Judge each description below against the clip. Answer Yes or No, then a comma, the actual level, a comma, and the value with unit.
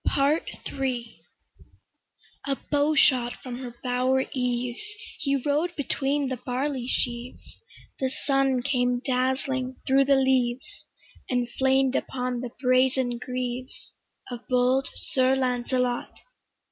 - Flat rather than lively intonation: Yes, narrow, 1.5 semitones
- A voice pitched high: Yes, very high, 255 Hz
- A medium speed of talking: No, slow, 115 wpm